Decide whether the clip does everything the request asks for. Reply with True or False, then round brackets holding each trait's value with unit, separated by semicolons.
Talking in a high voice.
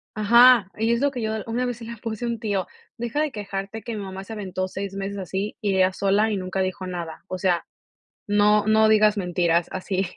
True (205 Hz)